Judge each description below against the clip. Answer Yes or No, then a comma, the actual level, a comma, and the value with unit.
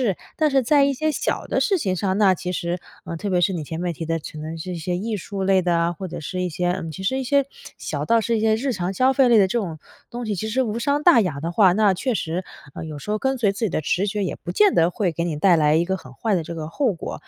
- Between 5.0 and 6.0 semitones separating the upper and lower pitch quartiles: Yes, average, 5.3 semitones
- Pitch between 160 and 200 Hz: Yes, high, 190 Hz